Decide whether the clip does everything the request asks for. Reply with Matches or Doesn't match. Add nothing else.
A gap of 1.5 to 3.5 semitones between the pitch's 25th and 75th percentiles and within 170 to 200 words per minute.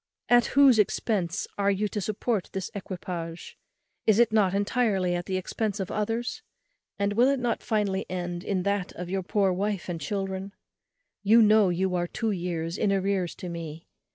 Matches